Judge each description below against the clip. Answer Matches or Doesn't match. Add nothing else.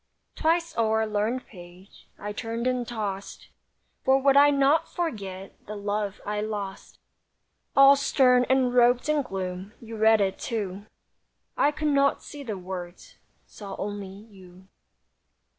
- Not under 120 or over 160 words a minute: Matches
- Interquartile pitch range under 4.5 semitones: Doesn't match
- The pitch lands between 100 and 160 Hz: Doesn't match